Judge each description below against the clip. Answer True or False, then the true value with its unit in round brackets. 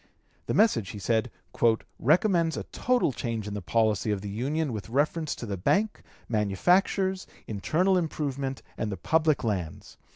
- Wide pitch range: True (7.7 semitones)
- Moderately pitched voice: False (130 Hz)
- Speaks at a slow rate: False (155 wpm)